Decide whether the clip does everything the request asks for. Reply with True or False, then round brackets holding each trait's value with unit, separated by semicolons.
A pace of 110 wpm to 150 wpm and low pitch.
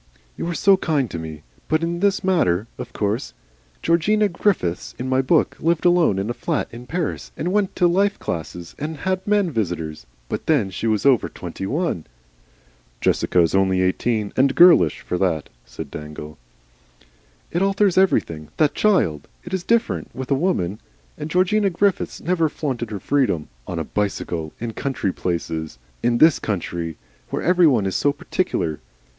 False (170 wpm; 130 Hz)